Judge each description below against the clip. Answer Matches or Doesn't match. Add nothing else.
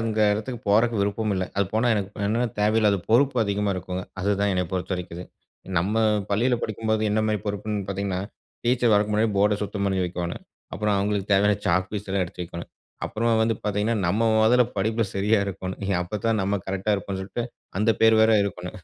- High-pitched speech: Doesn't match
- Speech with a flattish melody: Matches